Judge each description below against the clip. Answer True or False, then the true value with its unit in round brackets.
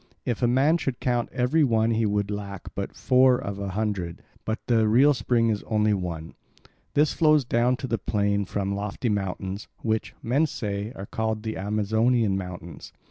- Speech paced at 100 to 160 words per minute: False (180 wpm)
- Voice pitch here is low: True (110 Hz)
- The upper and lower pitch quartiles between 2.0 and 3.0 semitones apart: False (3.5 semitones)